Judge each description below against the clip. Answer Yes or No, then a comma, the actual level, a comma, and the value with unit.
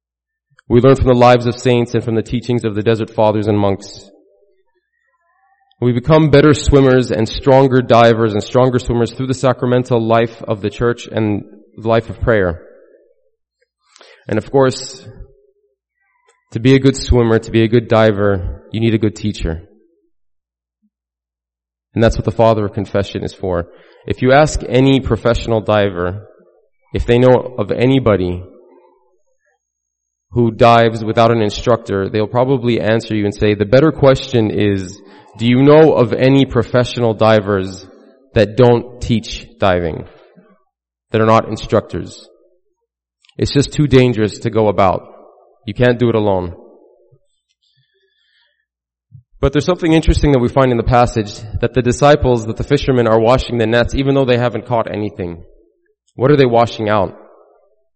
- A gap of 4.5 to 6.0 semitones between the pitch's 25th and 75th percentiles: No, average, 4.0 semitones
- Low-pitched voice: Yes, low, 115 Hz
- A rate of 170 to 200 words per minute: No, average, 155 wpm